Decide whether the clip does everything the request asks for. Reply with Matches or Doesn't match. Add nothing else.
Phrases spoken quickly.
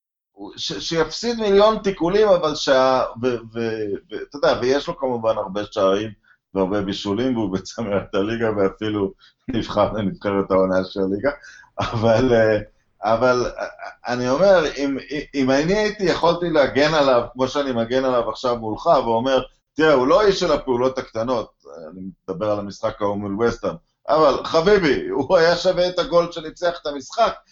Doesn't match